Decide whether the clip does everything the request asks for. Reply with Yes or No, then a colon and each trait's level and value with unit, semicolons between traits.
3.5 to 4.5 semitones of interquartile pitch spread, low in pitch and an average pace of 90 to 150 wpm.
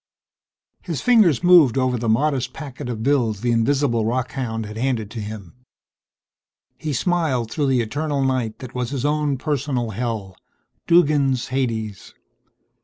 Yes: average, 4.1 semitones; low, 130 Hz; average, 140 wpm